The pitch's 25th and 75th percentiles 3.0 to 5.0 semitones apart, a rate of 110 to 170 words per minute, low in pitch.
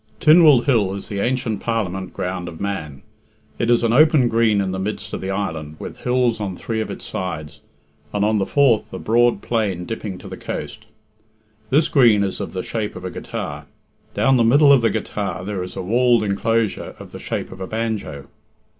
No: average, 4.0 semitones; fast, 205 wpm; low, 105 Hz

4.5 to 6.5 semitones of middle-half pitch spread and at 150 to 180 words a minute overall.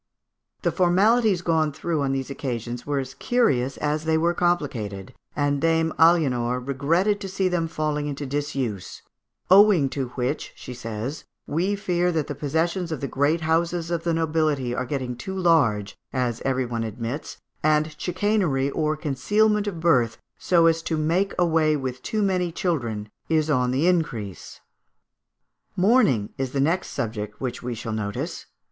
Yes: average, 5.1 semitones; average, 160 wpm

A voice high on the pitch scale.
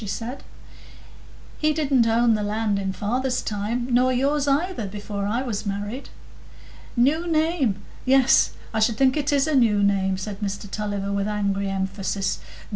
Yes: high, 220 Hz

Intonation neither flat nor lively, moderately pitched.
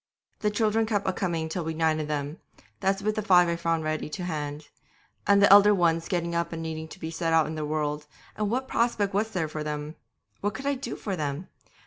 Yes: average, 4.5 semitones; medium, 170 Hz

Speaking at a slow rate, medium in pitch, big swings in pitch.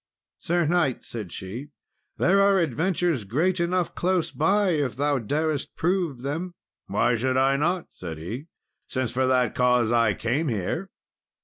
No: average, 150 wpm; medium, 145 Hz; wide, 6.2 semitones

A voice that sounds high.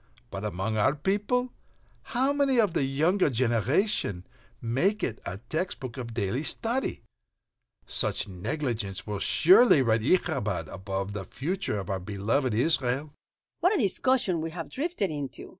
No: low, 135 Hz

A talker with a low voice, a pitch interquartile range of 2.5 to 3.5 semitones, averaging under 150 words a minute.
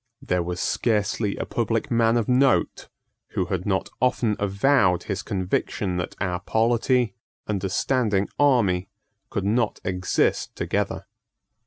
No: low, 100 Hz; average, 3.9 semitones; slow, 135 wpm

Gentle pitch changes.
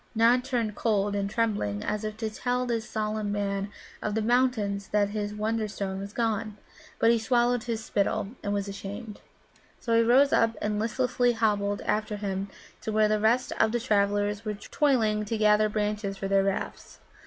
Yes: narrow, 2.0 semitones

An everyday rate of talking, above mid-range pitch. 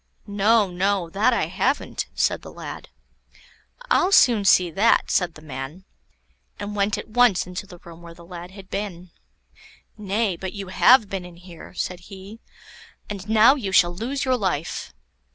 Yes: average, 170 wpm; high, 195 Hz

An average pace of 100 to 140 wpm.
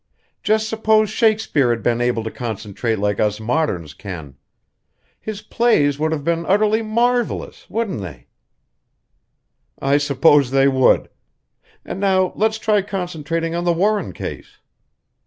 Yes: slow, 135 wpm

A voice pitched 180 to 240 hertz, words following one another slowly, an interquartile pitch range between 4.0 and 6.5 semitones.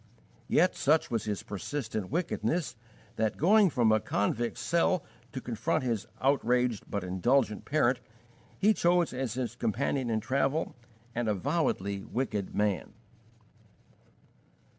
No: low, 125 Hz; slow, 120 wpm; average, 5.3 semitones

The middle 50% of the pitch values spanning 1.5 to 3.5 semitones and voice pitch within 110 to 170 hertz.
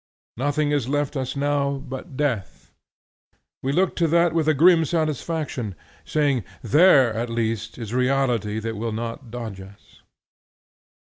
No: average, 4.5 semitones; low, 135 Hz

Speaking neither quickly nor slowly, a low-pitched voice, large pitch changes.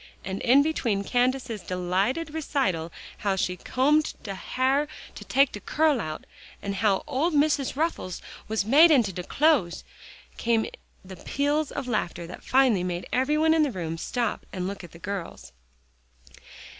No: average, 160 wpm; high, 235 Hz; wide, 7.5 semitones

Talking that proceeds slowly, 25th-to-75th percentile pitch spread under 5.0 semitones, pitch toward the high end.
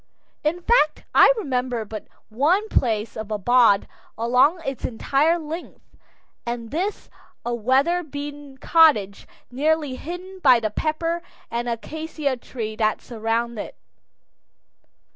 No: slow, 120 wpm; wide, 5.4 semitones; very high, 265 Hz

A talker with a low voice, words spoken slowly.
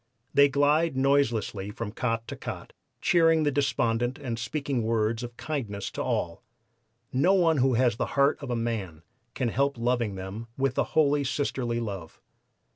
No: low, 125 Hz; average, 165 wpm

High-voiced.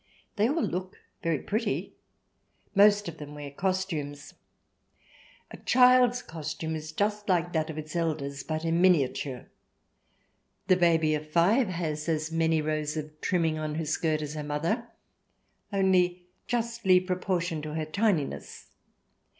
No: medium, 165 Hz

